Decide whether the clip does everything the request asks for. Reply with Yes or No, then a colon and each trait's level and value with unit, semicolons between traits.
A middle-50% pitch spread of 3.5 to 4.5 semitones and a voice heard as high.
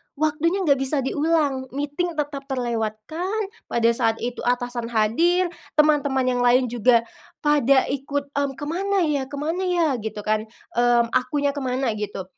Yes: average, 3.9 semitones; very high, 275 Hz